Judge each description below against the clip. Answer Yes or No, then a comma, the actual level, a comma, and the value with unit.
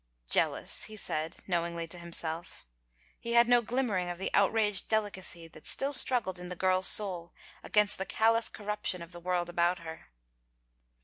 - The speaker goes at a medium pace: Yes, average, 170 wpm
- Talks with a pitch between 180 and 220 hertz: Yes, medium, 185 Hz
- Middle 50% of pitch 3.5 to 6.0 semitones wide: Yes, average, 3.8 semitones